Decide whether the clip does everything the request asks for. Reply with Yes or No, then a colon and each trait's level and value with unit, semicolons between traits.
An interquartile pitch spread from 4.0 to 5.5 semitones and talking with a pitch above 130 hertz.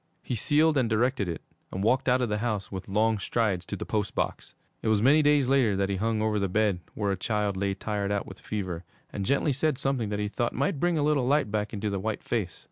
No: average, 4.3 semitones; low, 110 Hz